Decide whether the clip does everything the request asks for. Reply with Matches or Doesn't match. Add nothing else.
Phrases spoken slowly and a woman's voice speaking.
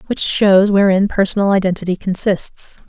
Matches